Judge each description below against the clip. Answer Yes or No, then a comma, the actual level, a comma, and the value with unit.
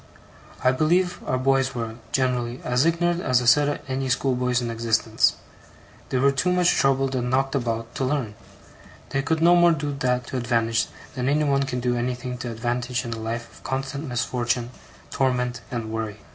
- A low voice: Yes, low, 125 Hz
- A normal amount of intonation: No, narrow, 2.3 semitones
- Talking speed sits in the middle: Yes, average, 185 wpm